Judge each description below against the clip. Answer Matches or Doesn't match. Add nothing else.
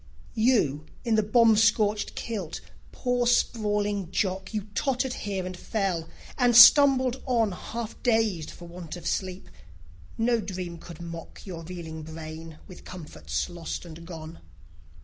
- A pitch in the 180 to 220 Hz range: Matches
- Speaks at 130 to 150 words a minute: Matches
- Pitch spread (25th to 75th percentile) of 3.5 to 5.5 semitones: Matches